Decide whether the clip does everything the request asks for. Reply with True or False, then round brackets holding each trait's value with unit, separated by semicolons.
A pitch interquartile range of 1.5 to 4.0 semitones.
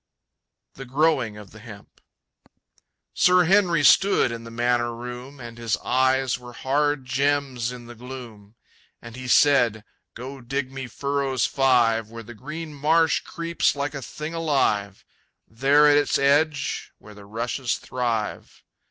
True (3.6 semitones)